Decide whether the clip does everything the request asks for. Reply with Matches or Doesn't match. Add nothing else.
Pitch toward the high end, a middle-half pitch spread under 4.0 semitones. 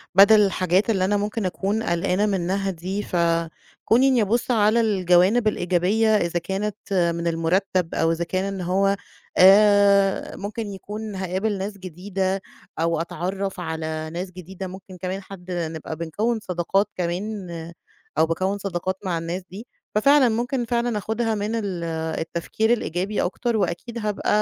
Matches